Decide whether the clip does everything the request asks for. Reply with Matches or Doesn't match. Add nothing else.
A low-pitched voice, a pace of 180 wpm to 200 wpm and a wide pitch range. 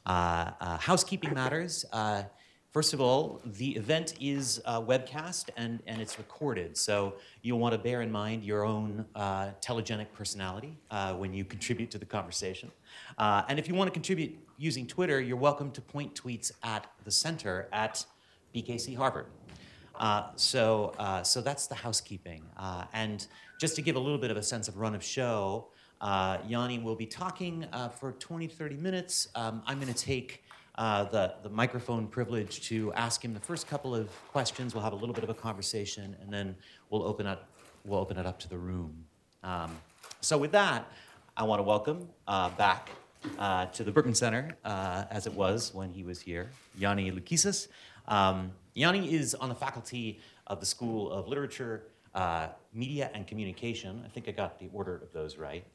Doesn't match